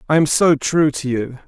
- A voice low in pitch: No, medium, 145 Hz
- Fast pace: Yes, fast, 245 wpm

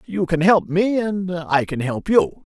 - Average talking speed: No, fast, 210 wpm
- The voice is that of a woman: No, male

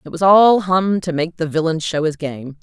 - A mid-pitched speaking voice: Yes, medium, 170 Hz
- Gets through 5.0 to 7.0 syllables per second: No, 4.8 syllables/s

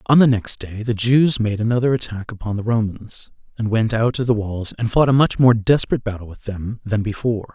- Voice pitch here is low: Yes, low, 110 Hz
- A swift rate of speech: Yes, fast, 230 wpm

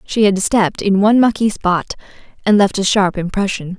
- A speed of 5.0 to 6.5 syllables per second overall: Yes, 5.5 syllables/s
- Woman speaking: Yes, female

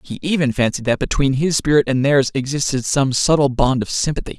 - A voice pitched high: No, low, 135 Hz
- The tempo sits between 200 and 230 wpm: Yes, fast, 205 wpm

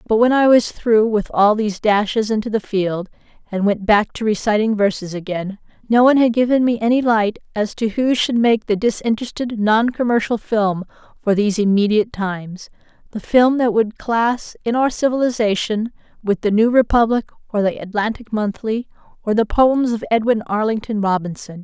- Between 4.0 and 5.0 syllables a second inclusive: No, 5.2 syllables/s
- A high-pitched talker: Yes, high, 220 Hz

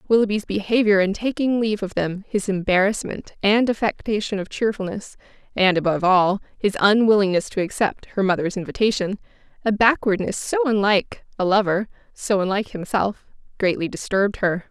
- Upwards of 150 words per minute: No, average, 145 wpm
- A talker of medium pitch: No, high, 205 Hz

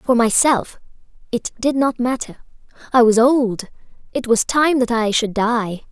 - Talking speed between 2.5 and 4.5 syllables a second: Yes, 4.1 syllables/s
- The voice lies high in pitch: Yes, high, 240 Hz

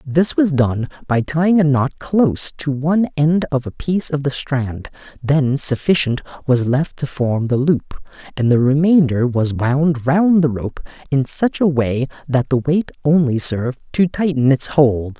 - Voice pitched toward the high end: No, medium, 140 Hz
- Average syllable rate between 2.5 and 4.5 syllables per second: Yes, 4.3 syllables/s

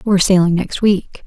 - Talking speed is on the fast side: No, average, 190 wpm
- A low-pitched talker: No, high, 190 Hz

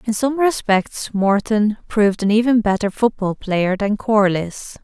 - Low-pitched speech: No, high, 210 Hz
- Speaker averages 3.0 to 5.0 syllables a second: Yes, 4.1 syllables/s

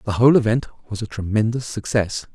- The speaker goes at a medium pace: Yes, average, 180 wpm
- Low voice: Yes, low, 110 Hz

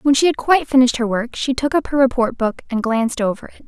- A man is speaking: No, female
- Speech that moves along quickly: Yes, fast, 280 wpm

